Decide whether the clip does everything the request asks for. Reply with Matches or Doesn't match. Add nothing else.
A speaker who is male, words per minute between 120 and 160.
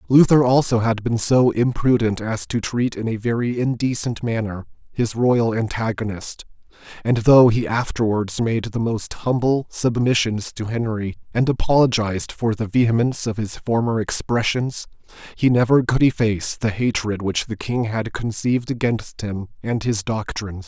Matches